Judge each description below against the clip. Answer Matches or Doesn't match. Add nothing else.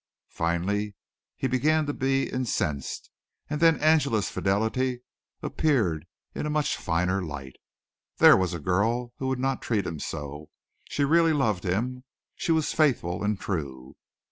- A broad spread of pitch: Matches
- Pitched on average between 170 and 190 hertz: Doesn't match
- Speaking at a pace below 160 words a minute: Matches